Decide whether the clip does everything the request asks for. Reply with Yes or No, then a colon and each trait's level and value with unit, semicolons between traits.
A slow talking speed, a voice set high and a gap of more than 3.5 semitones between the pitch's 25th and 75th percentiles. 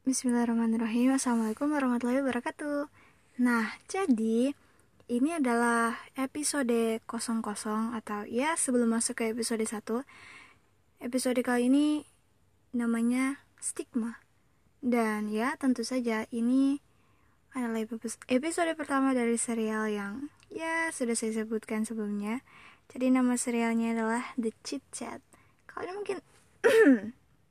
No: slow, 105 wpm; high, 240 Hz; average, 2.8 semitones